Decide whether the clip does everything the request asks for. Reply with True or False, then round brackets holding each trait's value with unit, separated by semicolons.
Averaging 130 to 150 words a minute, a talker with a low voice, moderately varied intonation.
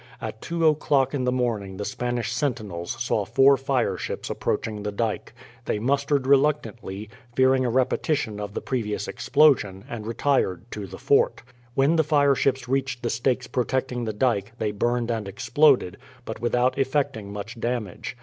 False (160 wpm; 125 Hz; 4.1 semitones)